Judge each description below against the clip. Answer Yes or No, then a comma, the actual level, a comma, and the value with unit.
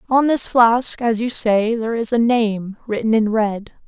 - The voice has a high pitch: Yes, high, 225 Hz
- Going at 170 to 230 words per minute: Yes, average, 200 wpm